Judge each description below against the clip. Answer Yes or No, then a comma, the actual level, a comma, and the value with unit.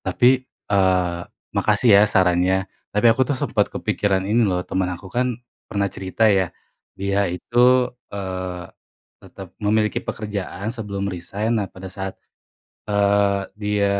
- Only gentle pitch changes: Yes, narrow, 1.9 semitones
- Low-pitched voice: Yes, low, 100 Hz